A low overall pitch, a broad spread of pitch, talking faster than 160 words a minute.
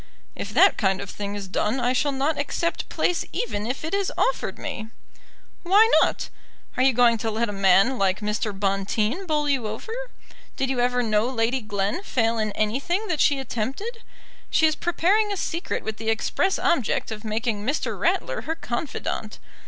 No: high, 245 Hz; wide, 6.6 semitones; average, 185 wpm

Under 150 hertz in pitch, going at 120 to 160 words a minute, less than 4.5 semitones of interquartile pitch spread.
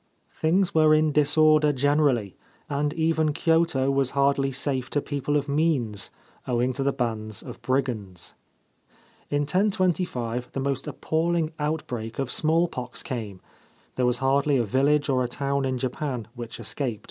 Yes: medium, 140 Hz; average, 145 wpm; average, 3.6 semitones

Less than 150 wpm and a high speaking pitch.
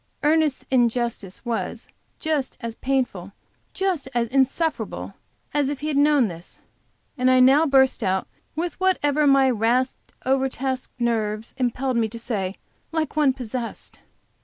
Yes: average, 140 wpm; very high, 260 Hz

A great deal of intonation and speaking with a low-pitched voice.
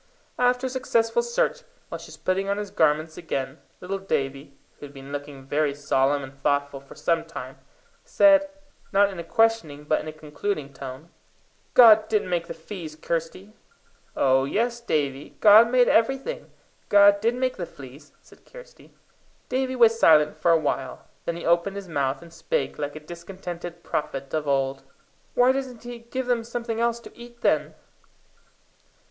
No: wide, 8.1 semitones; medium, 175 Hz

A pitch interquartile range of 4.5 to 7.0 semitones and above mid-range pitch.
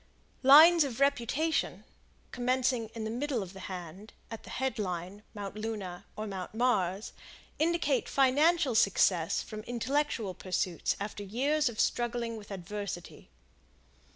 Yes: average, 5.1 semitones; high, 225 Hz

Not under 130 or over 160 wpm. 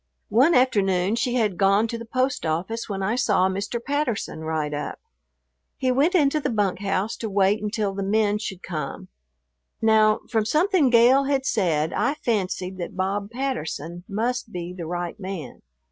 No: average, 170 wpm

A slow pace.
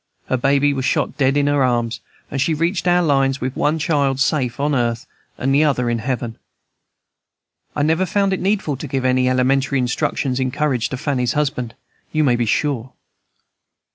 No: average, 185 wpm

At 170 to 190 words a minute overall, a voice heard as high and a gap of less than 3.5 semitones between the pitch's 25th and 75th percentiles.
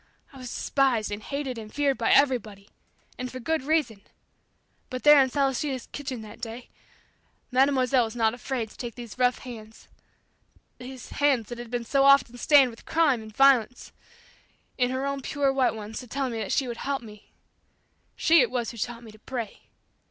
Yes: average, 185 wpm; very high, 250 Hz; average, 3.1 semitones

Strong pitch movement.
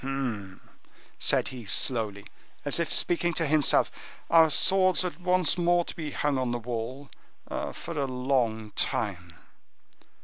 Yes: wide, 6.5 semitones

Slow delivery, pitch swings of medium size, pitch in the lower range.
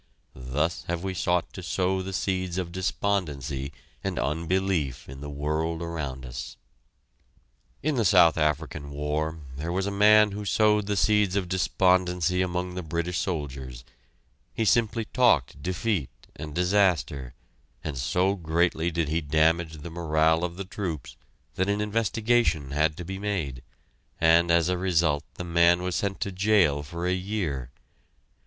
No: average, 155 wpm; average, 3.7 semitones; very low, 85 Hz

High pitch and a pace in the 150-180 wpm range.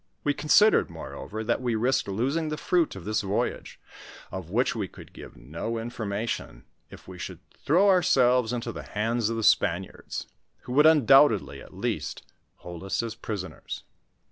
No: low, 115 Hz; average, 165 wpm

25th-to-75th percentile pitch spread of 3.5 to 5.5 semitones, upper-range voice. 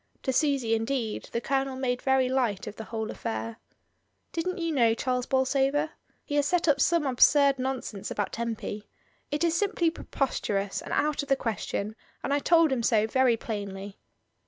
Yes: average, 4.2 semitones; very high, 260 Hz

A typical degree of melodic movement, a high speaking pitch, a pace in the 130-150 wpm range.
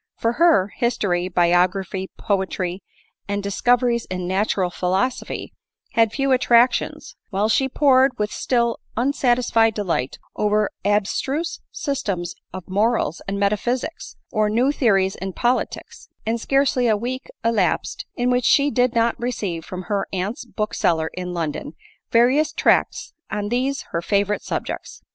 Yes: average, 4.5 semitones; high, 215 Hz; slow, 135 wpm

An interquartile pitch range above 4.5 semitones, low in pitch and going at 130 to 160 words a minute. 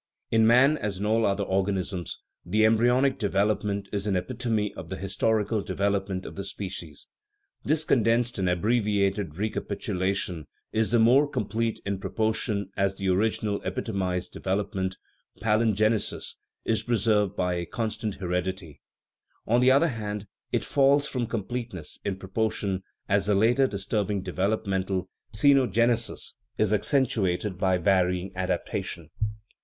No: average, 3.0 semitones; low, 105 Hz; average, 140 wpm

